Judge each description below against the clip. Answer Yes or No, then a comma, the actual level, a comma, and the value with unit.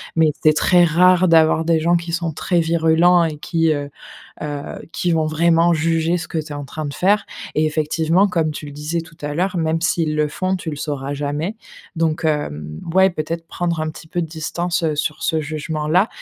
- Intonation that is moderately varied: No, narrow, 1.9 semitones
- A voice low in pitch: No, medium, 160 Hz